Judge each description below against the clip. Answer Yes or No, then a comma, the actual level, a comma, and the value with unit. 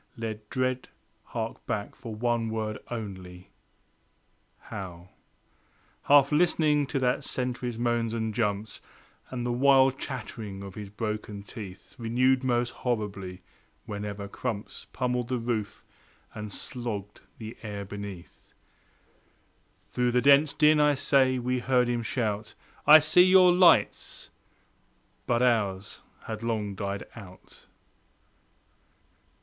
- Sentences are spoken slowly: Yes, slow, 120 wpm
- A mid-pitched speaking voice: No, low, 115 Hz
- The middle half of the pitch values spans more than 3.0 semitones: Yes, average, 3.7 semitones